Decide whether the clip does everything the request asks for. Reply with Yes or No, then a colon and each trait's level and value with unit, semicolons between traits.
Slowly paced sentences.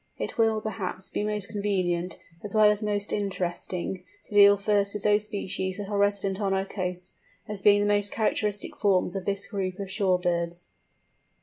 No: average, 185 wpm